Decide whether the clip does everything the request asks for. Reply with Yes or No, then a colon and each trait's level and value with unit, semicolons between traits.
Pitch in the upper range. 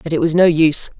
No: medium, 160 Hz